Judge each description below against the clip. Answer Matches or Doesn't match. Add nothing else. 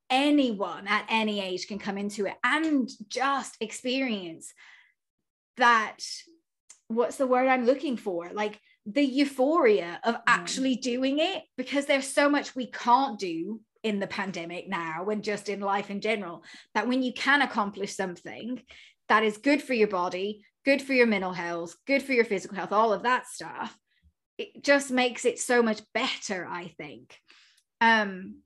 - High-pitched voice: Matches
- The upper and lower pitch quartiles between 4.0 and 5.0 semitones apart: Matches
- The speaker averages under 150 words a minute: Doesn't match